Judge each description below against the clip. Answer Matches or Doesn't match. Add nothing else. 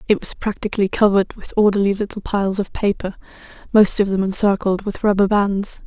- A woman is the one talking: Matches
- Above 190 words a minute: Doesn't match